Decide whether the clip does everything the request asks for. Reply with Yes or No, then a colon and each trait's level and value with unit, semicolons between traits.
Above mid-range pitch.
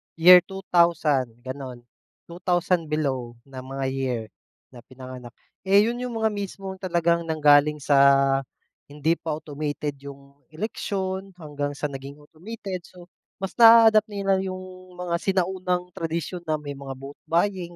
No: medium, 170 Hz